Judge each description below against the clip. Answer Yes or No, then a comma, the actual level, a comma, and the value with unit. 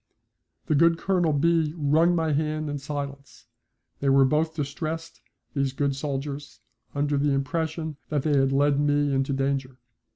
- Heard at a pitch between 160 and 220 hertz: No, medium, 145 Hz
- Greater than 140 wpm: Yes, average, 155 wpm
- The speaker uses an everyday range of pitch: No, narrow, 2.2 semitones